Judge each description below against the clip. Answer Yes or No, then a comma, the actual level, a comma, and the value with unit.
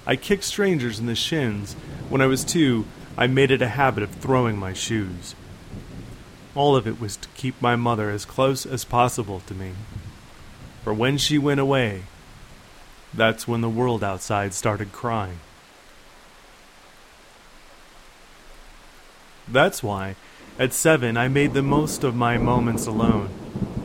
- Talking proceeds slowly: No, average, 145 wpm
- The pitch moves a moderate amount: Yes, average, 4.2 semitones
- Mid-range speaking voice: No, low, 115 Hz